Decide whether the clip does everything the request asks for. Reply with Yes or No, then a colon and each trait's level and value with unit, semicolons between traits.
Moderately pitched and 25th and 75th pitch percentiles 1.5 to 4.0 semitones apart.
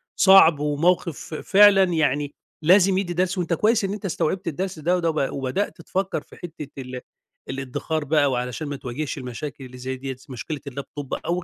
No: medium, 155 Hz; average, 4.9 semitones